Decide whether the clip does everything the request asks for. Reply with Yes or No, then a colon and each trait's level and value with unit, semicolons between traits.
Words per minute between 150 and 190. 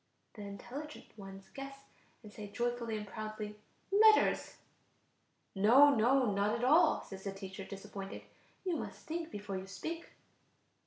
No: average, 140 wpm